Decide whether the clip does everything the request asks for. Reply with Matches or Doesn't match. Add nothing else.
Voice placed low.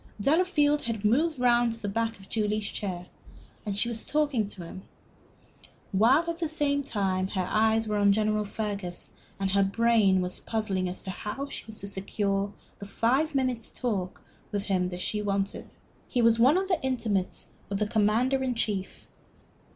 Doesn't match